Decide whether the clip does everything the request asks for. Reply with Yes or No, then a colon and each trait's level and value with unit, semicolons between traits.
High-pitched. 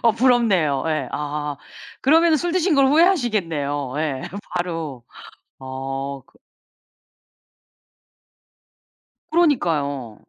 No: medium, 160 Hz